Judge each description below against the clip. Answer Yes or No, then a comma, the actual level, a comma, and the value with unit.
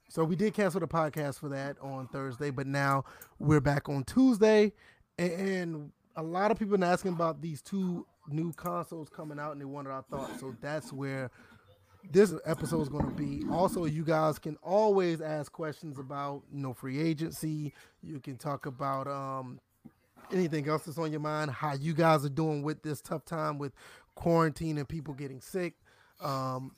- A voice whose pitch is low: No, medium, 155 Hz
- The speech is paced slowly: No, average, 190 wpm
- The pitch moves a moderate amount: Yes, average, 3.0 semitones